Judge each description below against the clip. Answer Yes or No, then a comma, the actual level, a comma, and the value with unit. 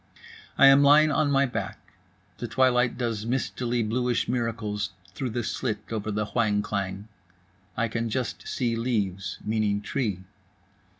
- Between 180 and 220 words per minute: No, average, 140 wpm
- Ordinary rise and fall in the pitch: Yes, average, 3.2 semitones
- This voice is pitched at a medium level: No, low, 115 Hz